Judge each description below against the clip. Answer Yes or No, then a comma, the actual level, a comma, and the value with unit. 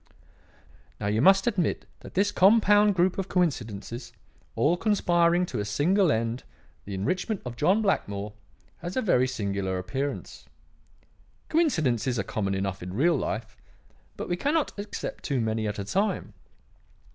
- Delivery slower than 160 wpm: Yes, average, 145 wpm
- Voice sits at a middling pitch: Yes, medium, 145 Hz